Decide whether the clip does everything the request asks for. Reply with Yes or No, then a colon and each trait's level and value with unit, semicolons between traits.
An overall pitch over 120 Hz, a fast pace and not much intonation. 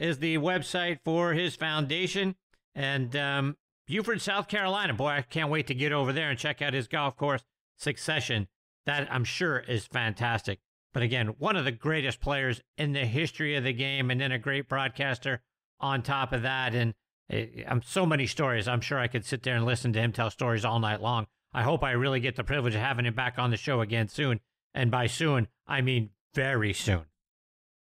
No: low, 135 Hz; fast, 210 wpm; average, 3.6 semitones